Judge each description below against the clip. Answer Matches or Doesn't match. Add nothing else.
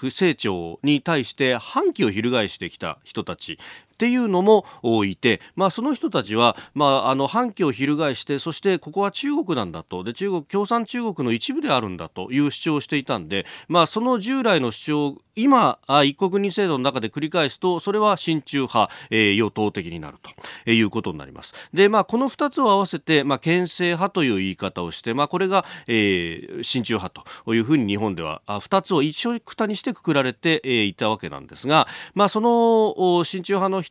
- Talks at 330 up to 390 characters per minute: Matches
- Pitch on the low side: Doesn't match